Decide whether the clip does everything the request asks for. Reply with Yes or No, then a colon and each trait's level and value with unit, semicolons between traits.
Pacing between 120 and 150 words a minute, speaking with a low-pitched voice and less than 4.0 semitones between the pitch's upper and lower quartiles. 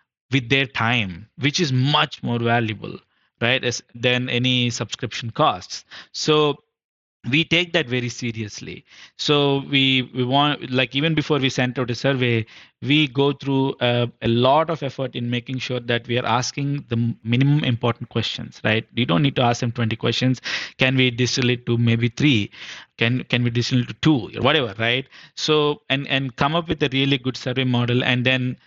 No: average, 190 wpm; low, 125 Hz; narrow, 2.6 semitones